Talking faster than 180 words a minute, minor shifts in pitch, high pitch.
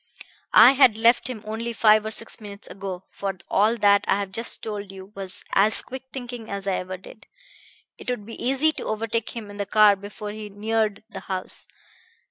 Yes: average, 200 wpm; narrow, 2.3 semitones; high, 215 Hz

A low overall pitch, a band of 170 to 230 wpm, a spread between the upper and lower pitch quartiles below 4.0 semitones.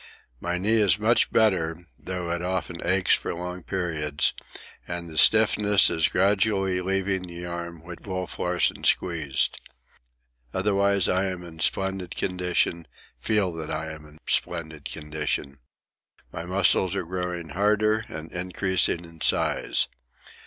No: very low, 90 Hz; slow, 135 wpm; narrow, 2.5 semitones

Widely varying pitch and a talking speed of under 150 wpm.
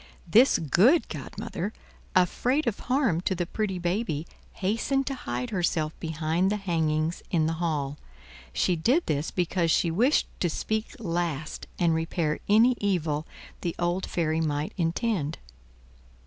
No: average, 4.8 semitones; average, 140 wpm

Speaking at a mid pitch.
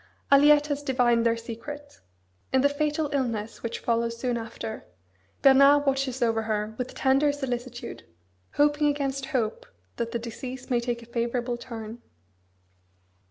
No: very high, 250 Hz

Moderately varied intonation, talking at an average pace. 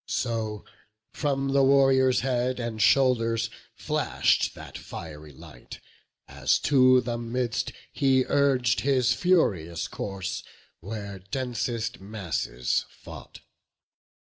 No: average, 4.5 semitones; slow, 100 wpm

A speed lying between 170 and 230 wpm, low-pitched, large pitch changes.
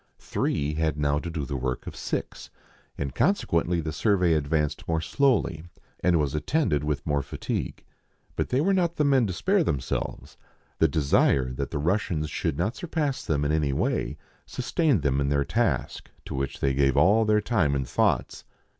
Yes: average, 185 wpm; very low, 80 Hz; wide, 7.1 semitones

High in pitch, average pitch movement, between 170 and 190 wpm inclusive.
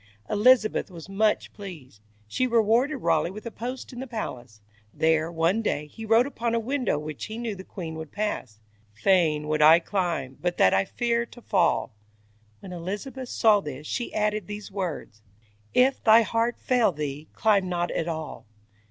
No: high, 195 Hz; wide, 6.3 semitones; average, 175 wpm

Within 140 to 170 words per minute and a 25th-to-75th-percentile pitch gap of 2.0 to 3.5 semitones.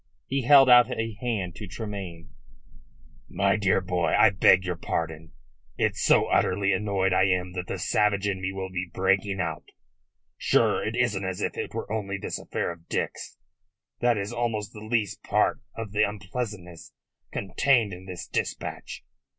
Yes: average, 165 wpm; average, 3.0 semitones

